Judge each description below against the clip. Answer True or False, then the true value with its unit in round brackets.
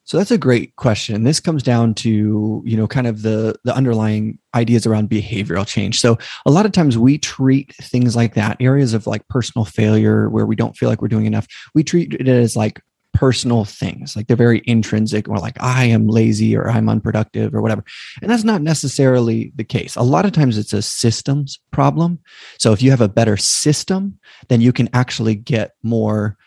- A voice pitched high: False (115 Hz)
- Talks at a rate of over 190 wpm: True (205 wpm)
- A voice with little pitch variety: False (3.2 semitones)